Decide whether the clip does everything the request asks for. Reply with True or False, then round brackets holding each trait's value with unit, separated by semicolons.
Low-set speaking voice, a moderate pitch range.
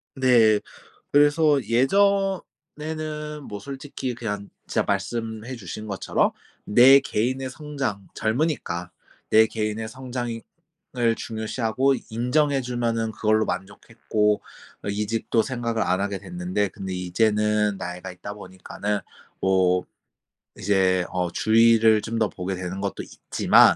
True (110 Hz; 4.4 semitones)